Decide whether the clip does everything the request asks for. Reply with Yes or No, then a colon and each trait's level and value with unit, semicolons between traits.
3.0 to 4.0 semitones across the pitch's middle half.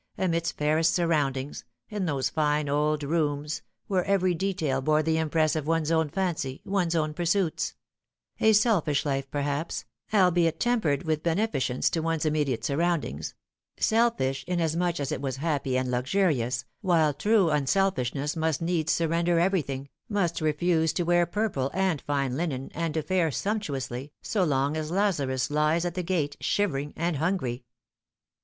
Yes: average, 3.6 semitones